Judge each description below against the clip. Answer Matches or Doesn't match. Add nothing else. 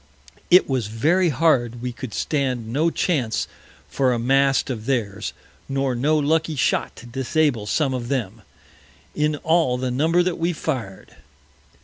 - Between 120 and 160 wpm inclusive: Matches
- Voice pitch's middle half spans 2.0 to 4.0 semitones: Doesn't match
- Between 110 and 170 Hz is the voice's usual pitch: Matches